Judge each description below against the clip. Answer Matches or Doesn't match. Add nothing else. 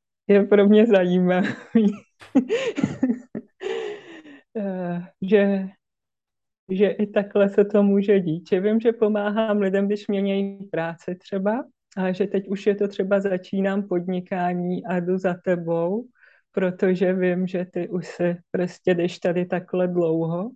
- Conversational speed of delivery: Matches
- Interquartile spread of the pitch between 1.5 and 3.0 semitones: Matches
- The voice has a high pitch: Matches